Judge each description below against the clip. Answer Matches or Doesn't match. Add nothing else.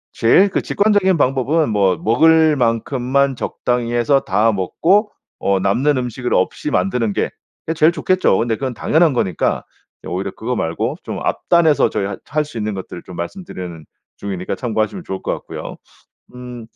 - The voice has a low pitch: Matches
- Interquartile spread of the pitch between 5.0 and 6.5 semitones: Doesn't match